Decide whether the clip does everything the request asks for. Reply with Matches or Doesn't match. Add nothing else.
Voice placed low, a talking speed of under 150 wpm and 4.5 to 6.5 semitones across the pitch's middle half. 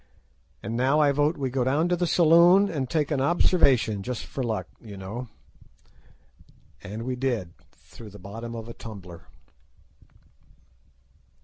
Matches